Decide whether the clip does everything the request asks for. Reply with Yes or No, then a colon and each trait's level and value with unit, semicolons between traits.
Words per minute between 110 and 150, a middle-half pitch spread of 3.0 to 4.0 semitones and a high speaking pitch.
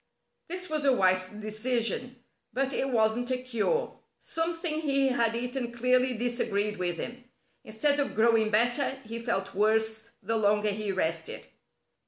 Yes: average, 145 wpm; average, 3.3 semitones; high, 235 Hz